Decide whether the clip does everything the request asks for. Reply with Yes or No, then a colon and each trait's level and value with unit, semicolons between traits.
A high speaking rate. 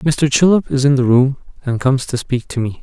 Yes: fast, 255 wpm